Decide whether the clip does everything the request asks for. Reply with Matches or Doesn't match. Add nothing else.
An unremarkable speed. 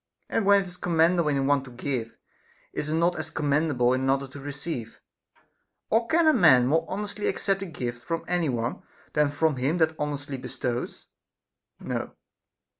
Matches